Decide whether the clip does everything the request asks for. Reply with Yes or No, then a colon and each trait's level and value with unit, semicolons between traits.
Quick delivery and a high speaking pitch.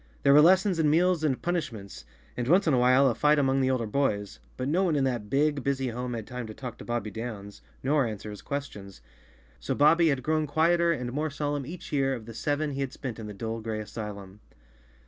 No: fast, 230 wpm; low, 135 Hz